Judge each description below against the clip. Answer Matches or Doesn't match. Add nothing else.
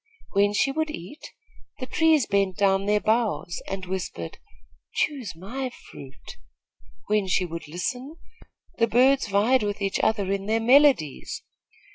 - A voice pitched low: Doesn't match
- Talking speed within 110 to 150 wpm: Matches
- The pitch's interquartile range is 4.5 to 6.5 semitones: Matches